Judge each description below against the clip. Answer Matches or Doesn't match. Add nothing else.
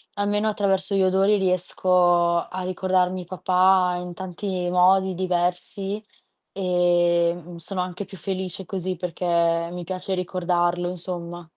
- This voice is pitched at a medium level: Matches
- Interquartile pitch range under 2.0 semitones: Matches